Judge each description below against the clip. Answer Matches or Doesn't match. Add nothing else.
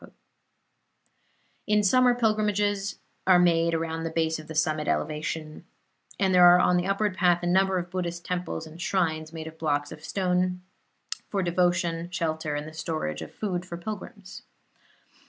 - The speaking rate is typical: Matches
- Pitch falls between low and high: Matches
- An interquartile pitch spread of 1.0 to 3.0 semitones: Matches